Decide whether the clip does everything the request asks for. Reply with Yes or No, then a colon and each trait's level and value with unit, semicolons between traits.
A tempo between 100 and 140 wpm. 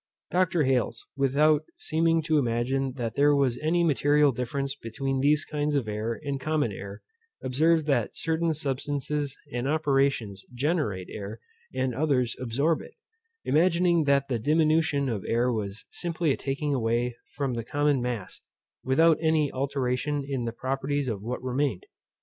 No: average, 150 wpm